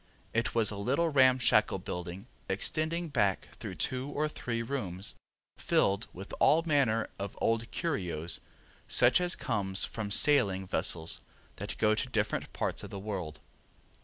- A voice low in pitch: Yes, low, 110 Hz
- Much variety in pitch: Yes, wide, 6.0 semitones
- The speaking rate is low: No, average, 145 wpm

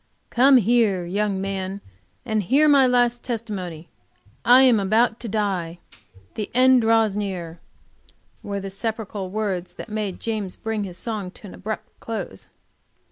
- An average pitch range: Yes, average, 3.3 semitones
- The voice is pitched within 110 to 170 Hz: No, high, 210 Hz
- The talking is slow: No, average, 145 wpm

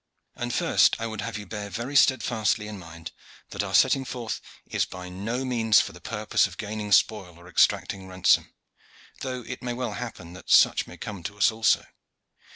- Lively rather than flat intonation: No, average, 3.8 semitones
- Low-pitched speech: Yes, low, 105 Hz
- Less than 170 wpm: No, average, 190 wpm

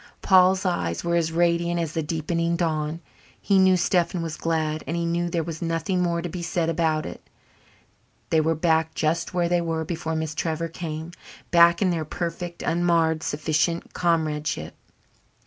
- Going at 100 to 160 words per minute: No, average, 170 wpm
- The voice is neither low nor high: Yes, medium, 165 Hz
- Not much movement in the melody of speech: Yes, narrow, 1.4 semitones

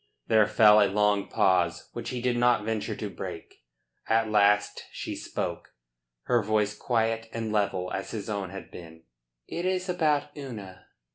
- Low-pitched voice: Yes, low, 110 Hz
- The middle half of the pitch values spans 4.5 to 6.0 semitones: No, average, 3.2 semitones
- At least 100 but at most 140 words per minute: No, average, 160 wpm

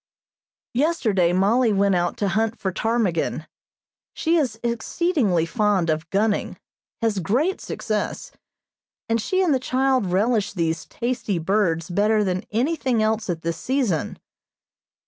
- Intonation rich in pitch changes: No, average, 5.0 semitones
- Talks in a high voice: Yes, high, 215 Hz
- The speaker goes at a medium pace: No, slow, 130 wpm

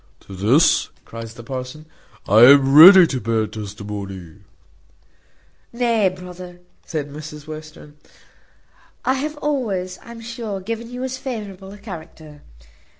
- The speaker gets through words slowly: Yes, slow, 125 wpm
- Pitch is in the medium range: Yes, medium, 165 Hz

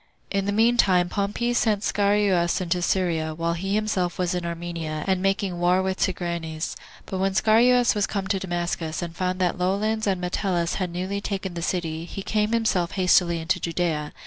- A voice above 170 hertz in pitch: Yes, medium, 185 Hz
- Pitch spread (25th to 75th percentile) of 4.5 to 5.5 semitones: No, average, 2.7 semitones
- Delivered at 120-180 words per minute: No, average, 190 wpm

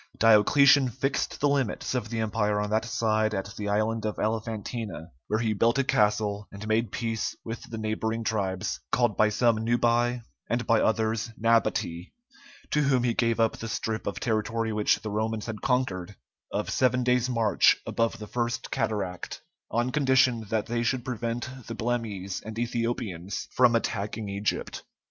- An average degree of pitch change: No, narrow, 2.0 semitones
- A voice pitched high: No, low, 115 Hz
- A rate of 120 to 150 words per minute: No, average, 165 wpm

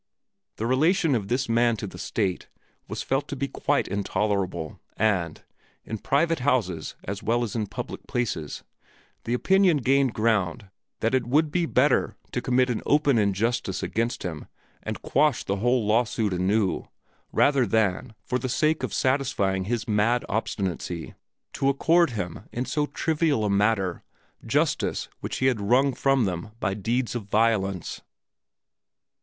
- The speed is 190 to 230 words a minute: No, average, 155 wpm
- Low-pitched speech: Yes, low, 115 Hz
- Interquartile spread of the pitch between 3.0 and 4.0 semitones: No, average, 4.9 semitones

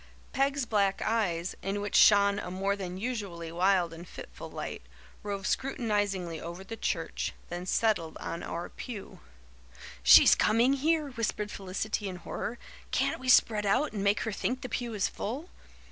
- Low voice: No, high, 205 Hz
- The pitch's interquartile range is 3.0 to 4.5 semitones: Yes, average, 3.8 semitones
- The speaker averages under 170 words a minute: Yes, average, 160 wpm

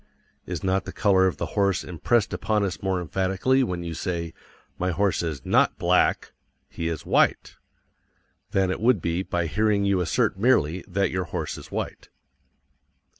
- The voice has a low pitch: Yes, very low, 95 Hz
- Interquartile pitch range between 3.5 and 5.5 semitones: No, narrow, 2.6 semitones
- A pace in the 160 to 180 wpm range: Yes, average, 170 wpm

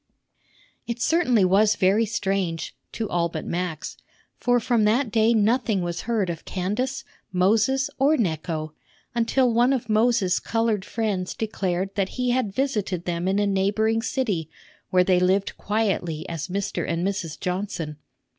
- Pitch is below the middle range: No, high, 205 Hz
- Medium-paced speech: Yes, average, 150 wpm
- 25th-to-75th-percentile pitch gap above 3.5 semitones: Yes, average, 4.0 semitones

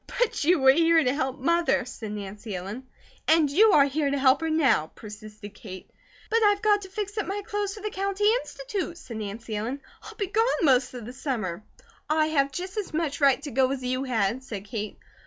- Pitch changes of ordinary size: No, wide, 8.2 semitones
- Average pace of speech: No, fast, 215 wpm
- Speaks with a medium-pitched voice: No, very high, 275 Hz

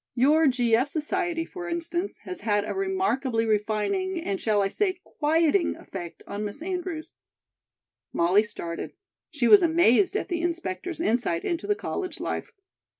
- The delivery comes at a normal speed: Yes, average, 155 wpm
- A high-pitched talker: Yes, very high, 315 Hz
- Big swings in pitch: Yes, wide, 8.4 semitones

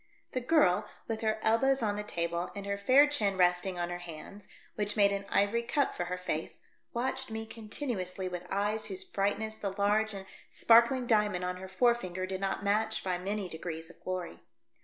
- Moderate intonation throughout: Yes, average, 3.2 semitones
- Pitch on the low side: No, high, 200 Hz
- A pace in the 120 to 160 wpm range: No, average, 195 wpm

